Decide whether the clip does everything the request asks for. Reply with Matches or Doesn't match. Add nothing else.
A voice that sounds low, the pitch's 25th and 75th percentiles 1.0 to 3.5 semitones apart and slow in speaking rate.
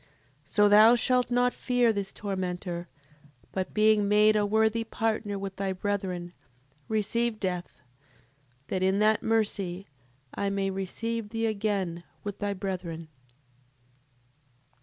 Doesn't match